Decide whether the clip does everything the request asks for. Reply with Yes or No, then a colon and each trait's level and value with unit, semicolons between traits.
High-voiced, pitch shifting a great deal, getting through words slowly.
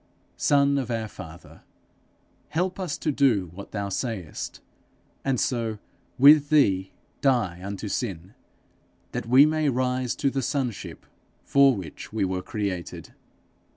No: low, 120 Hz; wide, 6.1 semitones; slow, 130 wpm